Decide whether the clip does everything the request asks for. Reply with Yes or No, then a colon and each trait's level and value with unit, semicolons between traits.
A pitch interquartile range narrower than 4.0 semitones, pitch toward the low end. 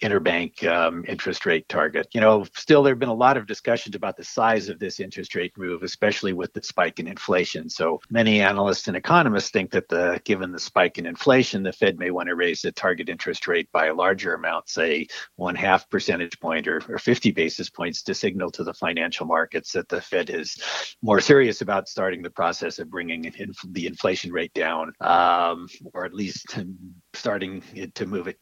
Yes: average, 3.2 semitones; very low, 90 Hz